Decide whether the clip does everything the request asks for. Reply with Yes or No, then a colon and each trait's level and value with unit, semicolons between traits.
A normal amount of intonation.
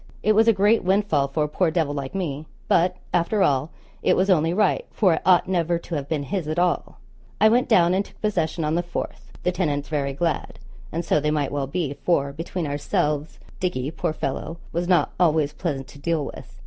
Yes: average, 3.7 semitones